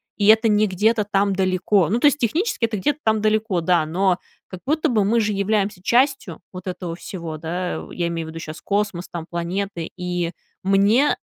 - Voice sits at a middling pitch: No, high, 195 Hz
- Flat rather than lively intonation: No, average, 3.6 semitones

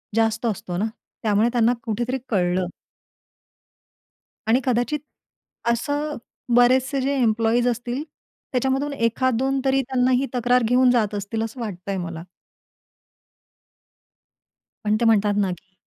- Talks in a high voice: Yes, high, 235 Hz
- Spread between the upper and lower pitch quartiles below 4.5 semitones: Yes, average, 3.2 semitones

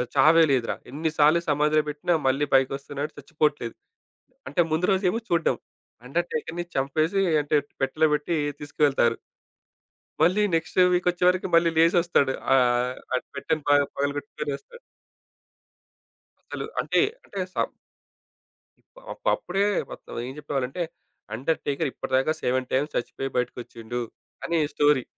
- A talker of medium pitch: Yes, medium, 150 Hz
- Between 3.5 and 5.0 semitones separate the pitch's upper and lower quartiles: Yes, average, 3.9 semitones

